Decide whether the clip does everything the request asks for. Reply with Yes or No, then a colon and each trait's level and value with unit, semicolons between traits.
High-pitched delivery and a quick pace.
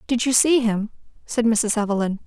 No: high, 225 Hz; average, 185 wpm